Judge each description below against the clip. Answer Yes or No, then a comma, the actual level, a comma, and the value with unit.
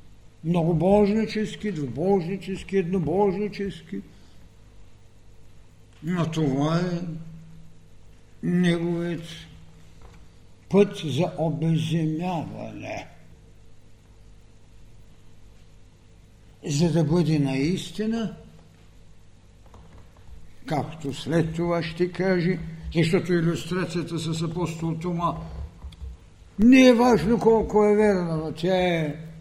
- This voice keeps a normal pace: No, slow, 65 wpm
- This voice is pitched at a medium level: Yes, medium, 160 Hz